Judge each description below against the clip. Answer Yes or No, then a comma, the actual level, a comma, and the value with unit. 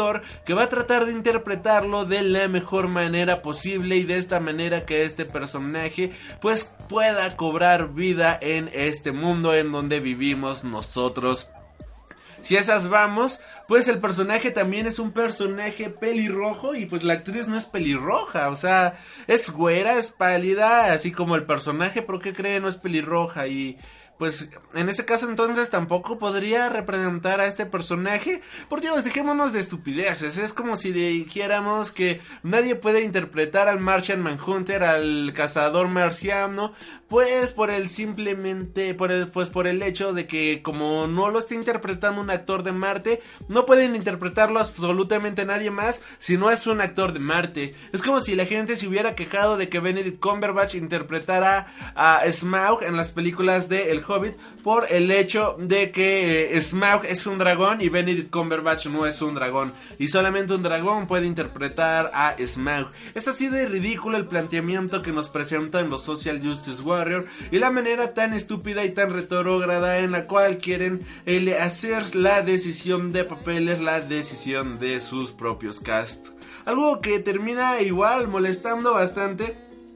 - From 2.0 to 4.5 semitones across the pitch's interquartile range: Yes, average, 4.2 semitones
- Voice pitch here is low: No, medium, 185 Hz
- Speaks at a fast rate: No, average, 165 wpm